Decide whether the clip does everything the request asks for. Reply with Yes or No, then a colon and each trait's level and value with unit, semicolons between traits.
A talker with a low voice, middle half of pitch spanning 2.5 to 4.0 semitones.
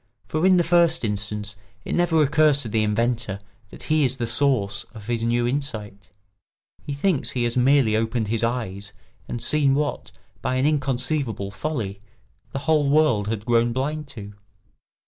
No: low, 125 Hz; average, 4.9 semitones